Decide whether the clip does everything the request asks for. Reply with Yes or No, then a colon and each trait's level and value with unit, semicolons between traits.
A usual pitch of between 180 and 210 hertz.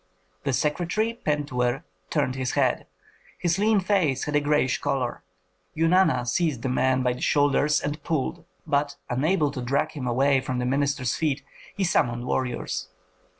No: medium, 145 Hz